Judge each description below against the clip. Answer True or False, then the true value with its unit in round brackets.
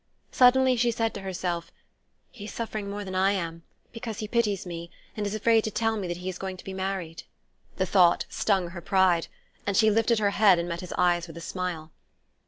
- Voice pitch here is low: False (190 Hz)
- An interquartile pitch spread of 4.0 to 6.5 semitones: False (3.6 semitones)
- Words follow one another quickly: True (215 wpm)